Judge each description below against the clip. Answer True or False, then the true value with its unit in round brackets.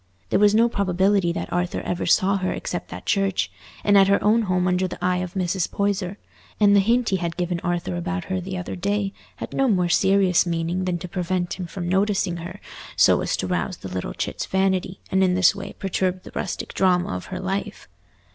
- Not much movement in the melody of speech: True (1.8 semitones)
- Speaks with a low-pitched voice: False (185 Hz)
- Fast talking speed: True (215 wpm)